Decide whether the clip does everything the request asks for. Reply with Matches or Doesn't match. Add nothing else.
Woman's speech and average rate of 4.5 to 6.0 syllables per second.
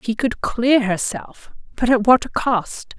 Doesn't match